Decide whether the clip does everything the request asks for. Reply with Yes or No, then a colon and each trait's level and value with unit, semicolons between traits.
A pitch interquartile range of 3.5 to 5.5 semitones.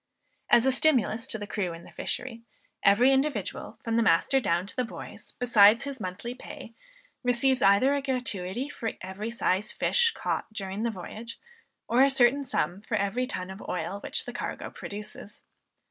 Yes: average, 4.4 semitones